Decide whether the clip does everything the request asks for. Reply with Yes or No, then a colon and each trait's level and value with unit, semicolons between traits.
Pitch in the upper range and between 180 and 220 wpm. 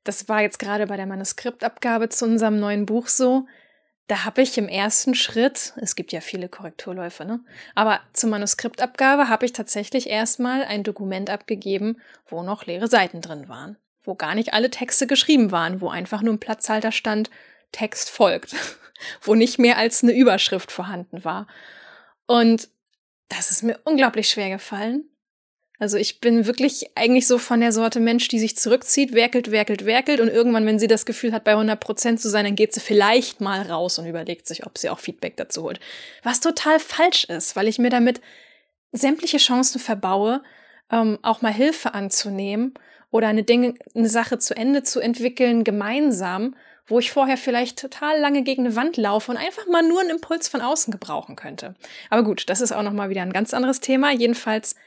Yes: high, 230 Hz; fast, 190 wpm